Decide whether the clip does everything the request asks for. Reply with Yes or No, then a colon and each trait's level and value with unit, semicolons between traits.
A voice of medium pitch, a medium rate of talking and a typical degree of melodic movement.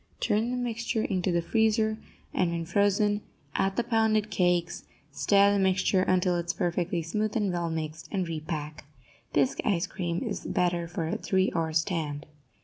Yes: medium, 180 Hz; average, 170 wpm; average, 3.6 semitones